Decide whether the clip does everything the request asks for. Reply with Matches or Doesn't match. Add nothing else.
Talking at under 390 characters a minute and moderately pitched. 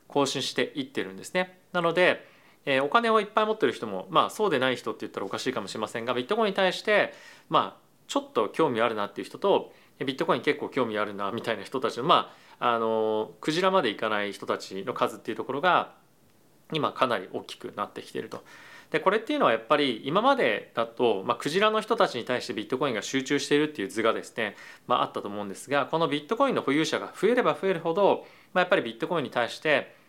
Doesn't match